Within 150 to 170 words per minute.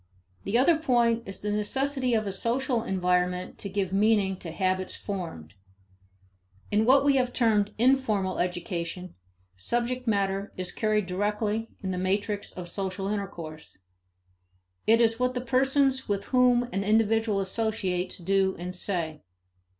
No: average, 140 wpm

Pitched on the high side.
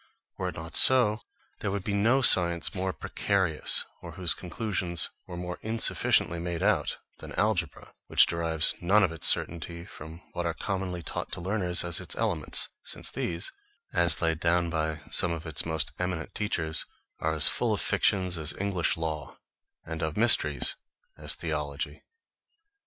No: very low, 85 Hz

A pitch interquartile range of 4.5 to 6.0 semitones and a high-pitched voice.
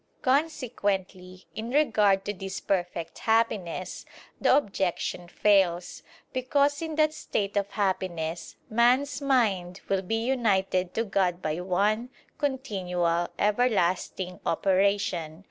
Yes: average, 4.9 semitones; high, 200 Hz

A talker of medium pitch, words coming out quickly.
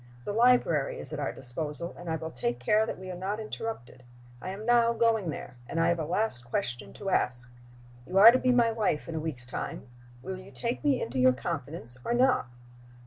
Yes: medium, 175 Hz; fast, 220 wpm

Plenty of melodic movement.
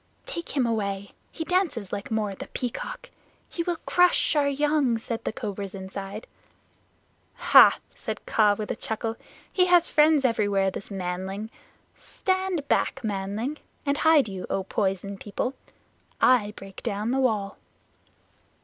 Yes: wide, 6.7 semitones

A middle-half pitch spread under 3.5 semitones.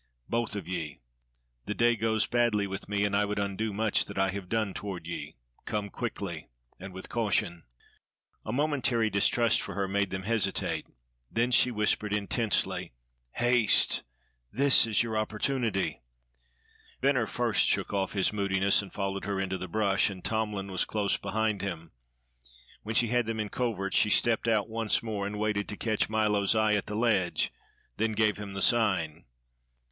Yes: narrow, 2.4 semitones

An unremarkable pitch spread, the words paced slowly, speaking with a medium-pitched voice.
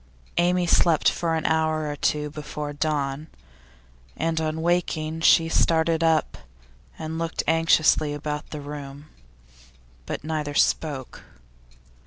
No: narrow, 1.6 semitones; slow, 120 wpm; medium, 155 Hz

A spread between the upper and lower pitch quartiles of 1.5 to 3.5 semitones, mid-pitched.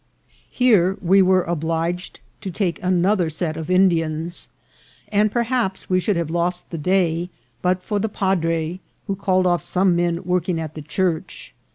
Yes: narrow, 2.4 semitones; medium, 180 Hz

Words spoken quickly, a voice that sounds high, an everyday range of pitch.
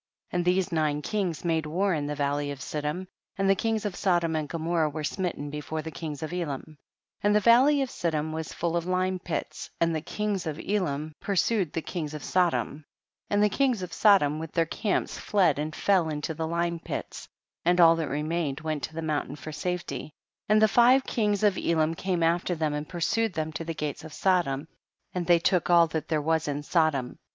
No: fast, 215 wpm; medium, 165 Hz; average, 3.3 semitones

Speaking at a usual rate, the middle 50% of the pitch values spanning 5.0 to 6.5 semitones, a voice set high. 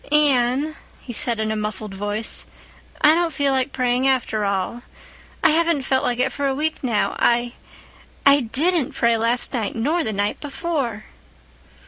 No: average, 160 wpm; average, 4.3 semitones; very high, 250 Hz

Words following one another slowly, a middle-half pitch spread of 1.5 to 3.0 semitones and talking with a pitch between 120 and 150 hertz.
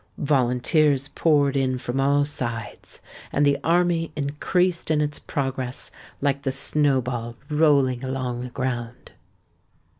Yes: slow, 120 wpm; average, 2.7 semitones; medium, 140 Hz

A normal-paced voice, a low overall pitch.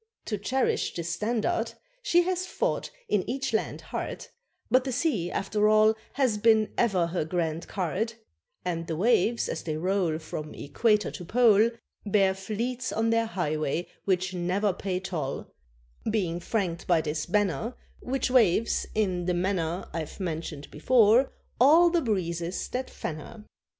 No: average, 150 wpm; high, 200 Hz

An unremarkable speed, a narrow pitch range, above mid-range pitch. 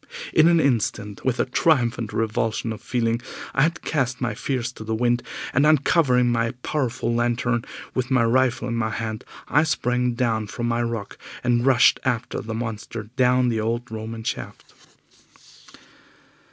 No: average, 160 wpm; narrow, 2.1 semitones; low, 120 Hz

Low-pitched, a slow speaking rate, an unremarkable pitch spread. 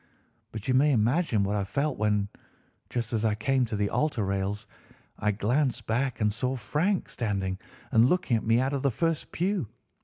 No: low, 115 Hz; average, 190 wpm; average, 4.6 semitones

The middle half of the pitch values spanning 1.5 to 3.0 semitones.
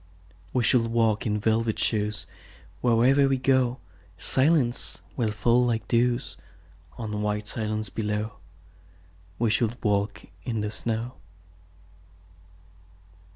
Yes: narrow, 2.4 semitones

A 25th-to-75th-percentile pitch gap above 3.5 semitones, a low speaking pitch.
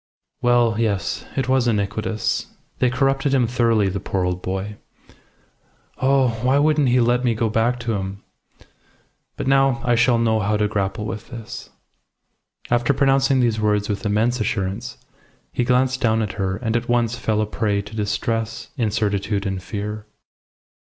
No: average, 2.9 semitones; low, 115 Hz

